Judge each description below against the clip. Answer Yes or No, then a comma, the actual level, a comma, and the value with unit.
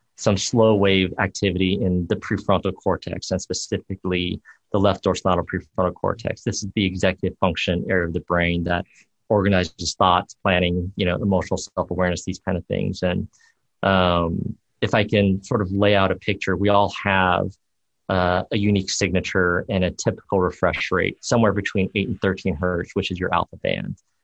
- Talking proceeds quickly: No, average, 175 wpm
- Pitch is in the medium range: No, very low, 95 Hz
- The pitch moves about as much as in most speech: No, narrow, 1.9 semitones